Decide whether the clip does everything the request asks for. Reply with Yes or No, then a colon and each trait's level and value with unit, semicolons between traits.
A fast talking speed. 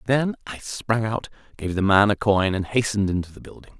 Yes: fast, 220 wpm